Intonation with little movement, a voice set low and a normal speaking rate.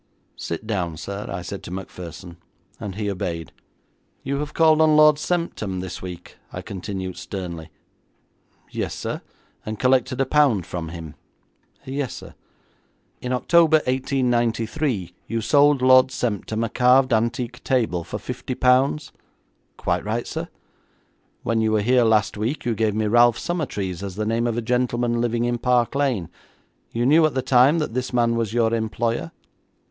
No: average, 4.3 semitones; low, 115 Hz; average, 160 wpm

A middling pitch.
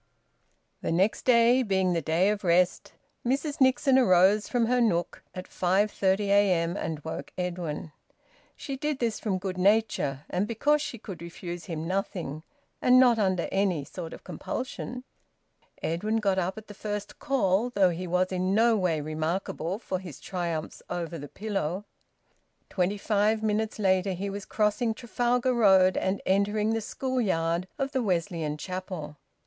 No: high, 195 Hz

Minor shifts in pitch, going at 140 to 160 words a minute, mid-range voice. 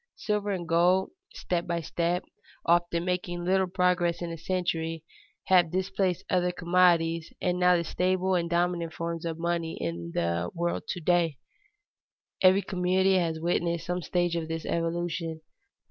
Yes: narrow, 1.4 semitones; average, 150 wpm; medium, 175 Hz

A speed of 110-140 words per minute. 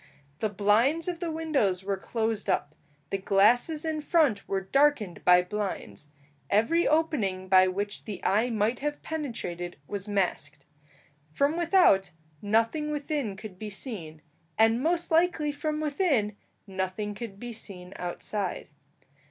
Yes: slow, 135 wpm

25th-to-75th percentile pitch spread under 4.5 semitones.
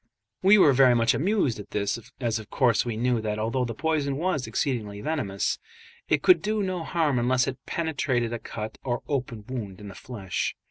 No: average, 5.2 semitones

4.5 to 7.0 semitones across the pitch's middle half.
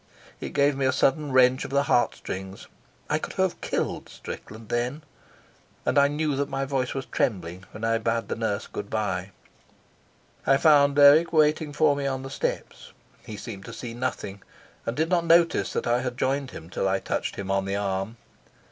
Yes: average, 5.1 semitones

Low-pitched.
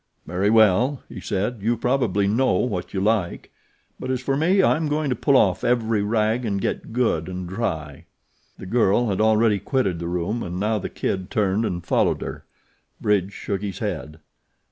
Yes: low, 105 Hz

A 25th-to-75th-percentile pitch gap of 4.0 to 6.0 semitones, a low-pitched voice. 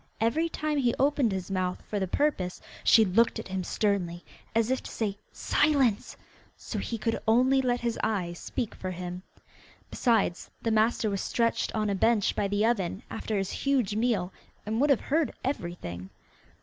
No: average, 4.4 semitones; high, 220 Hz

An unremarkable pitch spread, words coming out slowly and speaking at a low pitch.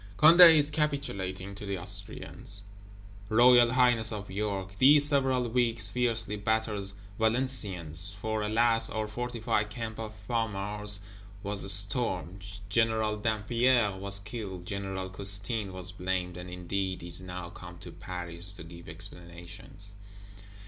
Yes: average, 3.3 semitones; slow, 125 wpm; low, 100 Hz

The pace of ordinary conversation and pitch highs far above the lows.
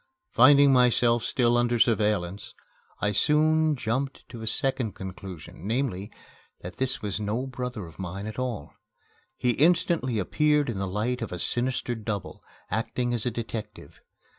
No: average, 150 wpm; average, 3.8 semitones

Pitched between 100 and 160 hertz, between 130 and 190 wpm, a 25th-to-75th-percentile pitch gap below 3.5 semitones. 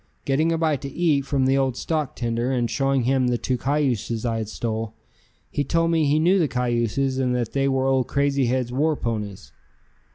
No: low, 135 Hz; fast, 205 wpm; average, 3.0 semitones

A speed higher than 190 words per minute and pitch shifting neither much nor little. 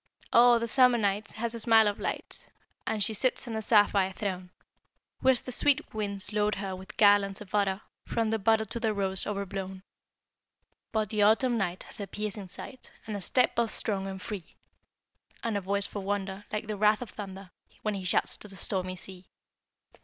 No: average, 200 wpm; narrow, 2.3 semitones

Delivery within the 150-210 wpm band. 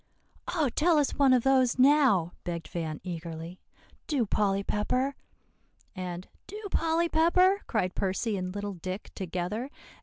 No: average, 140 wpm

